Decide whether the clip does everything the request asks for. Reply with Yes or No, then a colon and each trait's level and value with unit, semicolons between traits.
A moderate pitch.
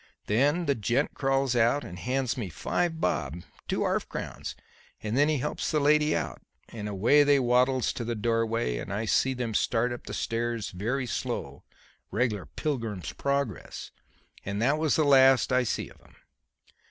No: low, 125 Hz